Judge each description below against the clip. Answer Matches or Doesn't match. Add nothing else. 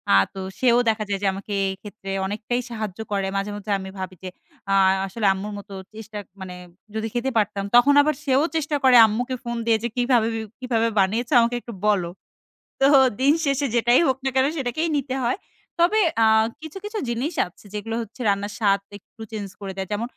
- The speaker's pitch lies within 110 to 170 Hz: Doesn't match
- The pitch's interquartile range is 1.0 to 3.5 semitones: Doesn't match